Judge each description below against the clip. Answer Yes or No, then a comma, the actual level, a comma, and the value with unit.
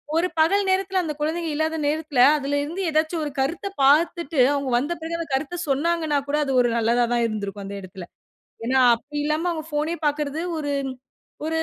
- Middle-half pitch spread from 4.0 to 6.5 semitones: No, average, 3.4 semitones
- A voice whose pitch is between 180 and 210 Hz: No, very high, 300 Hz